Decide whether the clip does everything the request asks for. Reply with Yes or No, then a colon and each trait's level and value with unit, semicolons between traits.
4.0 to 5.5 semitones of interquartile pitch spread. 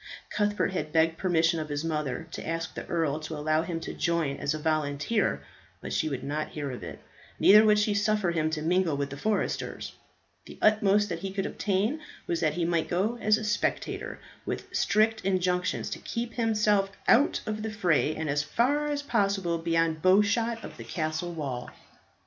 Yes: average, 5.1 semitones